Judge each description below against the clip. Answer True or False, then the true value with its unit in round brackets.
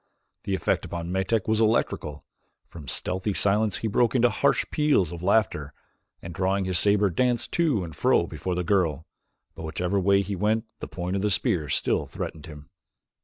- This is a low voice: True (95 Hz)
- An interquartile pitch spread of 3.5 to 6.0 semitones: True (4.0 semitones)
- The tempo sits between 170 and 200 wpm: True (180 wpm)